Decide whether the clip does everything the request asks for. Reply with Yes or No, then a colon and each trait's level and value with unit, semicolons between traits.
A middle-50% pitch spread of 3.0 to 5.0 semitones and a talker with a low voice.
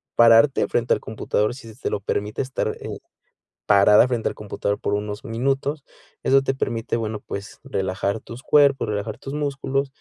Yes: average, 4.5 semitones; low, 115 Hz